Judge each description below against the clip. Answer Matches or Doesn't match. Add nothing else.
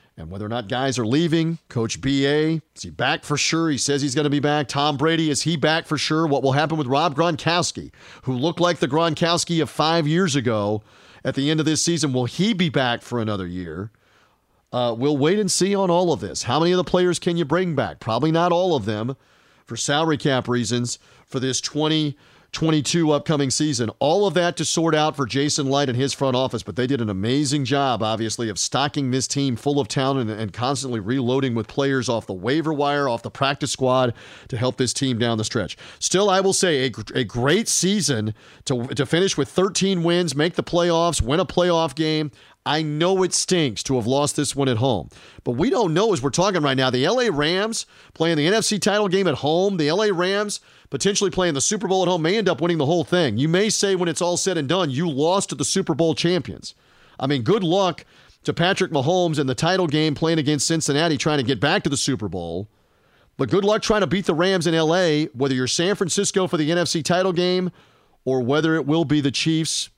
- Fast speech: Matches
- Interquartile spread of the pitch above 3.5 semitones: Matches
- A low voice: Doesn't match